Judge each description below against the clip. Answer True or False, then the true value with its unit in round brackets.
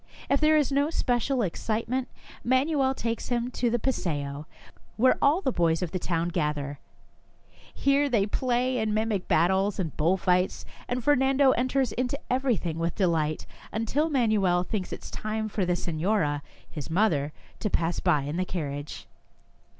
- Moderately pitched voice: False (215 Hz)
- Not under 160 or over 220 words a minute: True (165 wpm)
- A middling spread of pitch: False (7.1 semitones)